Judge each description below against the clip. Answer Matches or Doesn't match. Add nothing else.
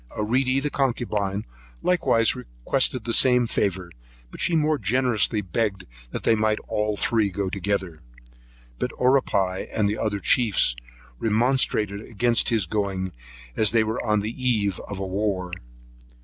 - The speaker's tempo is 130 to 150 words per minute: Matches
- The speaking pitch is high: Doesn't match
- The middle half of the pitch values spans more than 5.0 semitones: Doesn't match